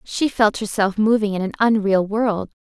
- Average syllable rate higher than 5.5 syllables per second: No, 4.6 syllables/s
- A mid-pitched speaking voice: No, high, 210 Hz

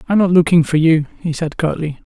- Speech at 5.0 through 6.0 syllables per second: No, 6.3 syllables/s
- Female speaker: No, male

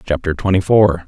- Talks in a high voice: No, very low, 90 Hz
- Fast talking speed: No, average, 165 wpm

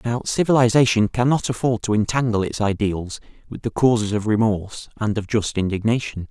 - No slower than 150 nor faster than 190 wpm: Yes, average, 160 wpm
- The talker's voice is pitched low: Yes, low, 110 Hz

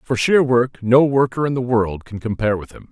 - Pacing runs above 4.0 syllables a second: Yes, 5.4 syllables/s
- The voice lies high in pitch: No, low, 120 Hz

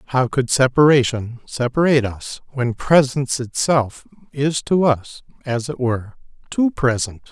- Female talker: No, male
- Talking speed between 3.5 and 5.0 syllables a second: Yes, 4.5 syllables/s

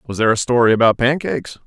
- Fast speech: Yes, fast, 215 wpm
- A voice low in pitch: Yes, low, 120 Hz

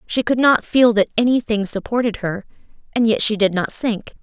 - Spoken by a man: No, female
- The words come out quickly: Yes, fast, 215 wpm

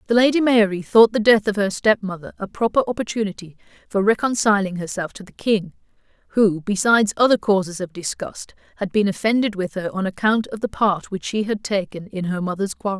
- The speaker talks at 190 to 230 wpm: Yes, average, 200 wpm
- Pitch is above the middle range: Yes, high, 205 Hz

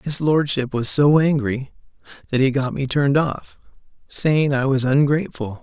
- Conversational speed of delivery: Yes, average, 160 wpm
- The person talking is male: Yes, male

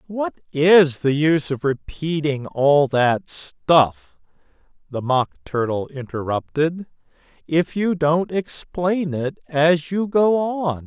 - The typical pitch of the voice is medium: Yes, medium, 160 Hz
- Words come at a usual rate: No, slow, 120 wpm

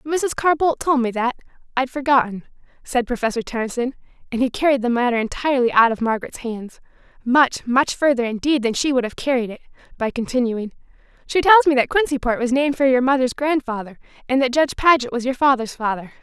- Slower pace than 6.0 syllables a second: No, 6.1 syllables/s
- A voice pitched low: No, very high, 255 Hz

